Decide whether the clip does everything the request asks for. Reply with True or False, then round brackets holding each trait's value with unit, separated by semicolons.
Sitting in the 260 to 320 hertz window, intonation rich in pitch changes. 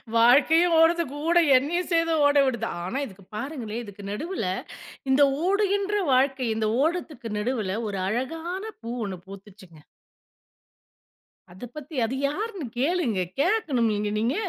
True (270 Hz; 7.3 semitones)